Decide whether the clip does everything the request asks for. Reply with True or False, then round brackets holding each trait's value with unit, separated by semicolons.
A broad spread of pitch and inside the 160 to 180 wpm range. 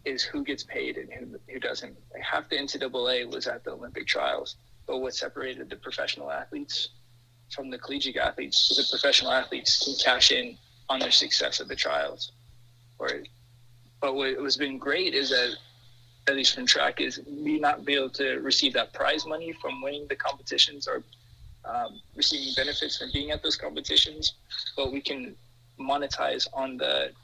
False (2.7 semitones; 175 wpm)